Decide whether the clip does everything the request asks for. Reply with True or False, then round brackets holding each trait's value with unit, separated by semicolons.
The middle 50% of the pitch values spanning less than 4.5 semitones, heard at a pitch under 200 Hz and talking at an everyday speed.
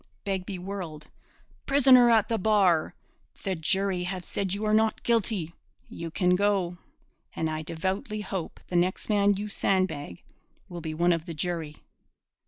True (3.4 semitones; 190 Hz; 155 wpm)